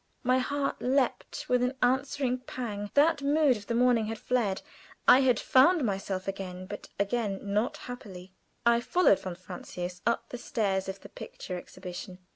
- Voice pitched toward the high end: Yes, high, 235 Hz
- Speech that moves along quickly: No, average, 165 wpm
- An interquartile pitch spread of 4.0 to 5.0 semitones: Yes, average, 4.7 semitones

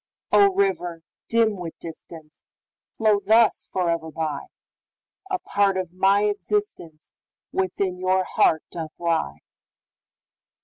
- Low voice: No, medium, 185 Hz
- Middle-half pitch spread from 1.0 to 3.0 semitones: No, average, 4.4 semitones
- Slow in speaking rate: Yes, slow, 90 wpm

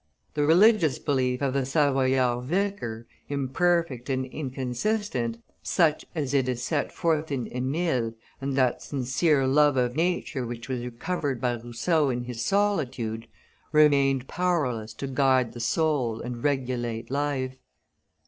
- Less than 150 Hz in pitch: Yes, low, 135 Hz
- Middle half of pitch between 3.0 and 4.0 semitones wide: Yes, average, 3.6 semitones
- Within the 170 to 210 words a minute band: No, slow, 135 wpm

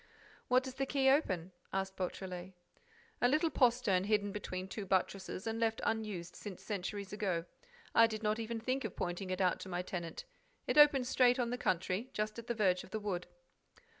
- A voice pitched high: Yes, high, 210 Hz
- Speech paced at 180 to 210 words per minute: Yes, average, 195 wpm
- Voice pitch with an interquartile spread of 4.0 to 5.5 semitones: Yes, average, 4.4 semitones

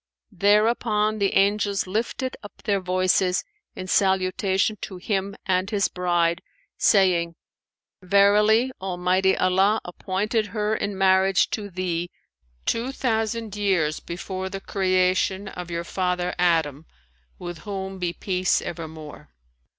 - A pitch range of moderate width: No, narrow, 2.2 semitones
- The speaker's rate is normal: No, slow, 120 wpm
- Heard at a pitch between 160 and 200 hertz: Yes, high, 190 Hz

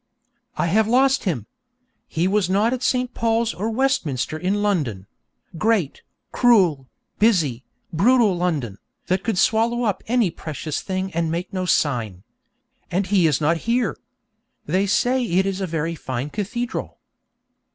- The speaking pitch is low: No, high, 190 Hz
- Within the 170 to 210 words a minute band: No, average, 145 wpm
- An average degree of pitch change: No, wide, 6.0 semitones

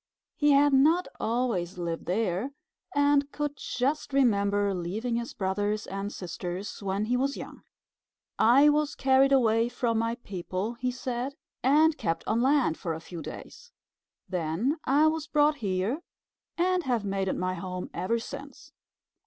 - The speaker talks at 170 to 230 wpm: No, average, 155 wpm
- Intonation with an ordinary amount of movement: No, wide, 6.6 semitones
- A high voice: Yes, high, 235 Hz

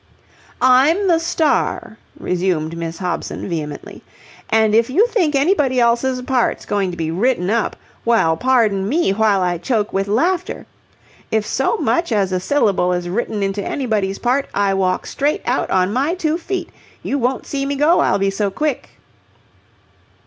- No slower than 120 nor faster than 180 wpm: Yes, average, 165 wpm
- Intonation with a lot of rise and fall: Yes, wide, 6.5 semitones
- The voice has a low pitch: No, high, 225 Hz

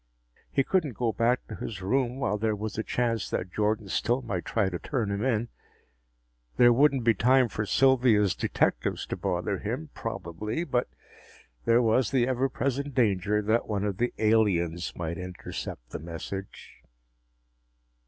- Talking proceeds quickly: No, average, 160 wpm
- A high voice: No, low, 110 Hz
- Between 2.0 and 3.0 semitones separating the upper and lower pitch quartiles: No, average, 4.0 semitones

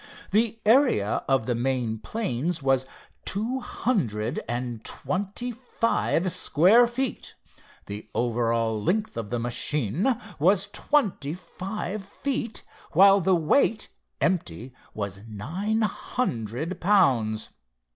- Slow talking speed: Yes, slow, 110 wpm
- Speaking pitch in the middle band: Yes, medium, 165 Hz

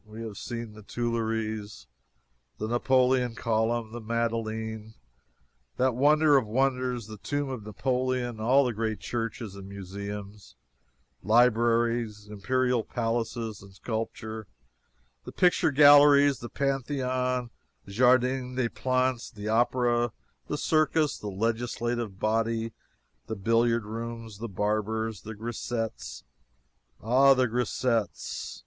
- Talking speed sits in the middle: No, slow, 115 wpm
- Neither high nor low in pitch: No, low, 115 Hz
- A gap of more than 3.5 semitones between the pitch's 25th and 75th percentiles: No, average, 2.7 semitones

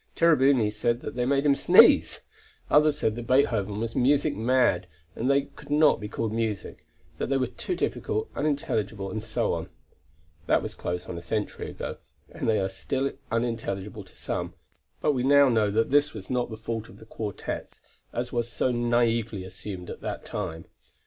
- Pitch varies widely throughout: No, average, 4.3 semitones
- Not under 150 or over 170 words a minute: No, average, 185 wpm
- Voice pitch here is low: Yes, low, 115 Hz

